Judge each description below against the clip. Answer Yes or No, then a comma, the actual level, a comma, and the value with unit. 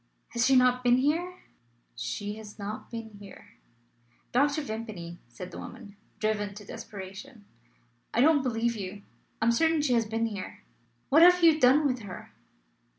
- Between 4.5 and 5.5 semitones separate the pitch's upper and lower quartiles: Yes, average, 4.8 semitones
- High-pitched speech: Yes, high, 230 Hz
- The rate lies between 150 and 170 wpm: Yes, average, 160 wpm